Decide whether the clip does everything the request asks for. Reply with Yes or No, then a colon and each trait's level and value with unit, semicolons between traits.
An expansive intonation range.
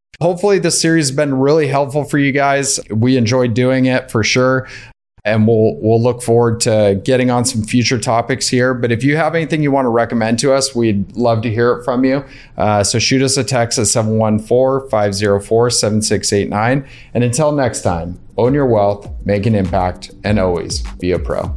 No: average, 3.7 semitones